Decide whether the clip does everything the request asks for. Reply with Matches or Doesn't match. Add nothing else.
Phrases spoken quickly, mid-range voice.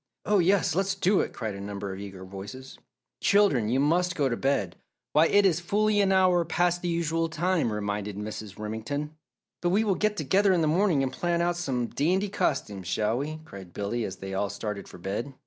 Matches